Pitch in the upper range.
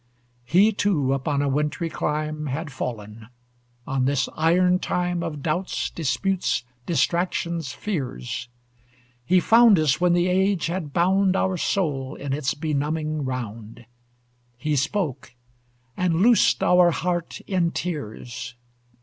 No: medium, 155 Hz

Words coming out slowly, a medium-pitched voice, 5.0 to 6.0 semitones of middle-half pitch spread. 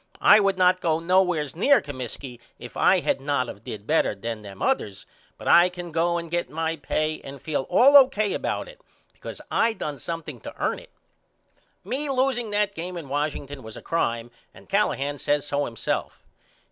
No: average, 185 wpm; medium, 165 Hz; wide, 5.6 semitones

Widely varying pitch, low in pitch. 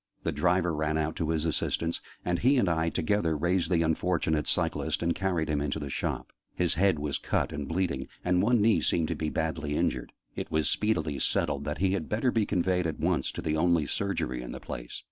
No: average, 3.0 semitones; very low, 80 Hz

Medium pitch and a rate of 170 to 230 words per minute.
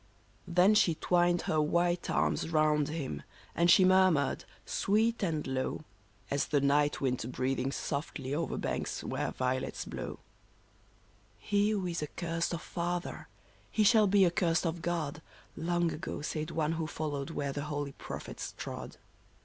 No: medium, 160 Hz; average, 150 wpm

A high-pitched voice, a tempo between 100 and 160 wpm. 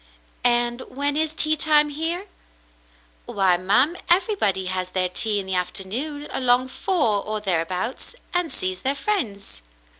Yes: high, 245 Hz; average, 140 wpm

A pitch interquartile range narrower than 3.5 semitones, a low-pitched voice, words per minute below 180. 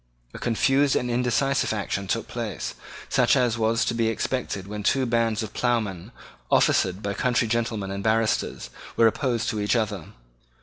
Yes: average, 2.8 semitones; low, 115 Hz; average, 165 wpm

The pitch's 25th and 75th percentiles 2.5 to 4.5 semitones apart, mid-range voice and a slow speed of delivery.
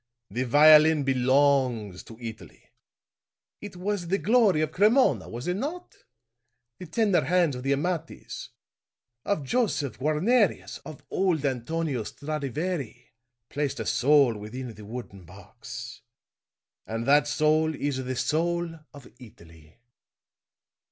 No: wide, 5.6 semitones; medium, 145 Hz; slow, 120 wpm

